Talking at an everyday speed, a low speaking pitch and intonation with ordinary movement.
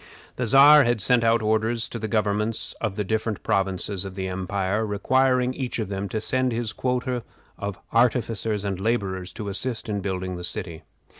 Yes: average, 180 wpm; low, 110 Hz; average, 3.5 semitones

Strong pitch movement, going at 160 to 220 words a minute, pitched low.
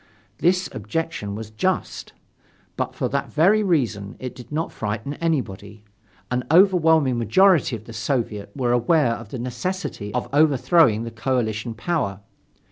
No: wide, 6.7 semitones; average, 140 wpm; low, 125 Hz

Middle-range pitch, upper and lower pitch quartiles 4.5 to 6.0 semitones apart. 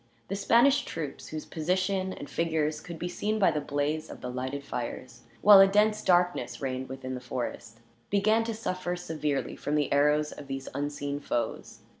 Yes: medium, 150 Hz; wide, 5.4 semitones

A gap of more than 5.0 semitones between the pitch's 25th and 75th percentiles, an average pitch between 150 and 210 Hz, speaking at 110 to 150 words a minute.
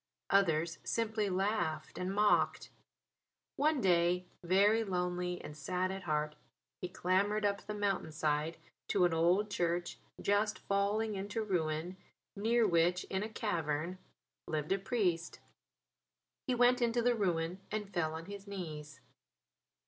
No: average, 3.6 semitones; medium, 185 Hz; slow, 135 wpm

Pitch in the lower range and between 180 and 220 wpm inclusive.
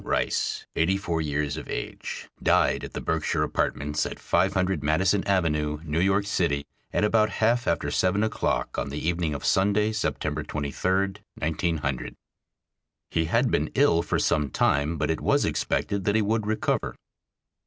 No: very low, 85 Hz; average, 160 wpm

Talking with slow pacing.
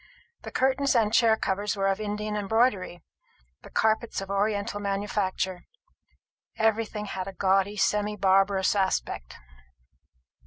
Yes: slow, 120 wpm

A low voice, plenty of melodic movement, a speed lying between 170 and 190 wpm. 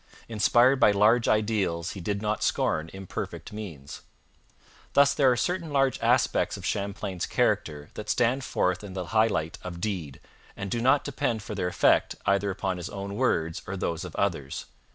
No: low, 100 Hz; average, 4.3 semitones; average, 175 wpm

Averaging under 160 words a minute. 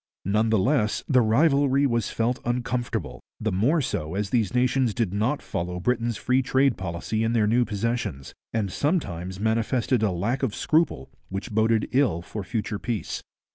No: average, 170 wpm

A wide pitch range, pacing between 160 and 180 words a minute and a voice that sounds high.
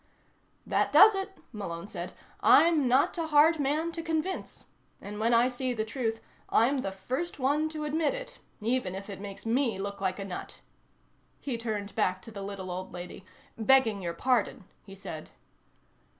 Yes: wide, 7.0 semitones; average, 175 wpm; high, 230 Hz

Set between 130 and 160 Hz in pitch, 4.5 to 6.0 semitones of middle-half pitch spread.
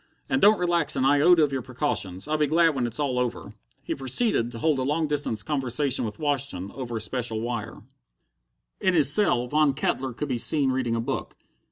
No: low, 135 Hz; average, 3.9 semitones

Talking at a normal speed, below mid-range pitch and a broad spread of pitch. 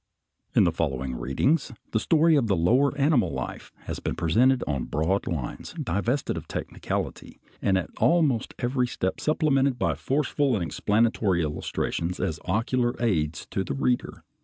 Yes: average, 150 wpm; low, 110 Hz; wide, 8.1 semitones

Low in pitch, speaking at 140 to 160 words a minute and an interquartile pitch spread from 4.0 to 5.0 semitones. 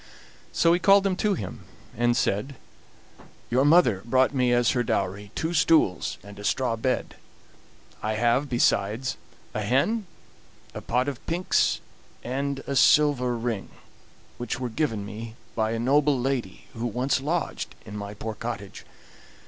Yes: low, 125 Hz; average, 150 wpm; average, 4.3 semitones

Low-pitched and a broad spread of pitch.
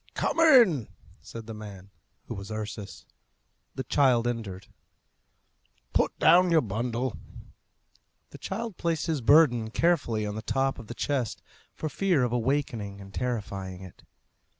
Yes: low, 120 Hz; wide, 5.8 semitones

